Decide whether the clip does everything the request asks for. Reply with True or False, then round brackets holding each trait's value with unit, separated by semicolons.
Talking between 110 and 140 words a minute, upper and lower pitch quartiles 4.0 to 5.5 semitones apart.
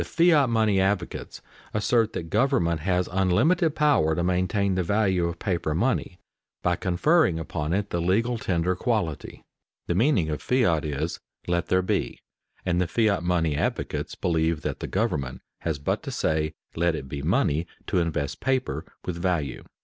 False (165 wpm; 4.6 semitones)